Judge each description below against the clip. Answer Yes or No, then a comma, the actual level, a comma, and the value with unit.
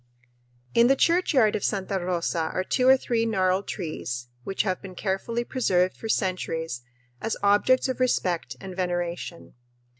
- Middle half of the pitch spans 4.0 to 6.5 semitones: Yes, average, 4.6 semitones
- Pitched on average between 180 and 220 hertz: Yes, high, 190 Hz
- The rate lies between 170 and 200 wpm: No, average, 150 wpm